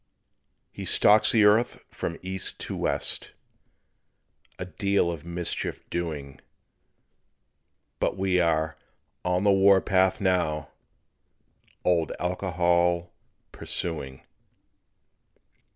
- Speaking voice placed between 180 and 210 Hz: No, very low, 90 Hz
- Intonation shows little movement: Yes, narrow, 2.3 semitones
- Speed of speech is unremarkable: No, slow, 90 wpm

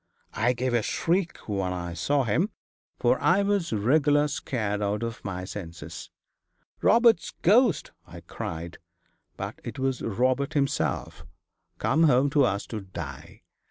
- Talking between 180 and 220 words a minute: No, average, 140 wpm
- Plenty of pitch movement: Yes, wide, 6.7 semitones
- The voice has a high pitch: No, low, 125 Hz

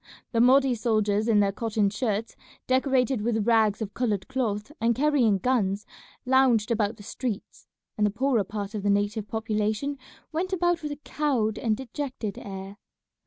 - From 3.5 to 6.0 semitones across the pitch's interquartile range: Yes, average, 3.9 semitones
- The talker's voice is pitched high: Yes, high, 225 Hz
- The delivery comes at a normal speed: Yes, average, 165 wpm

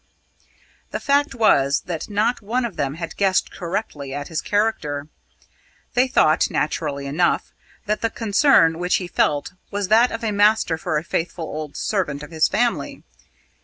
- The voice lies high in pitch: No, medium, 180 Hz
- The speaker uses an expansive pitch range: Yes, wide, 6.1 semitones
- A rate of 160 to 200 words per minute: Yes, average, 165 wpm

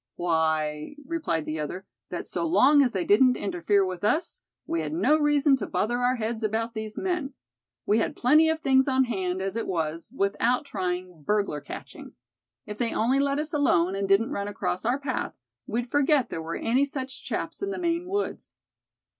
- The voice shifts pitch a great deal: Yes, wide, 7.1 semitones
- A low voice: No, high, 225 Hz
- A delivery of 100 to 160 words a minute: No, average, 190 wpm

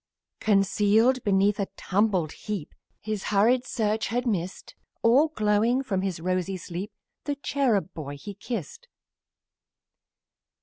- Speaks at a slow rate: Yes, slow, 120 wpm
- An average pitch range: Yes, average, 3.7 semitones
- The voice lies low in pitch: No, high, 210 Hz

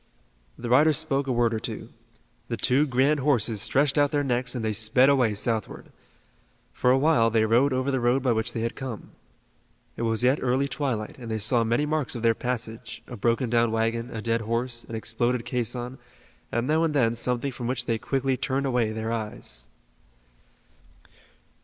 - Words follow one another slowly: No, average, 190 wpm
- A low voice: Yes, low, 120 Hz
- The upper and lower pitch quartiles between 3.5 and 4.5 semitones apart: No, average, 2.7 semitones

